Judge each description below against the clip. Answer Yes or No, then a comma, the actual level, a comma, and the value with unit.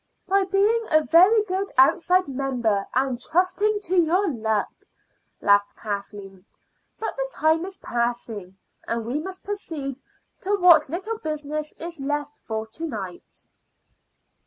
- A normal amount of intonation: No, wide, 8.0 semitones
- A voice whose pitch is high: Yes, very high, 305 Hz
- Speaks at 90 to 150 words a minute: Yes, slow, 135 wpm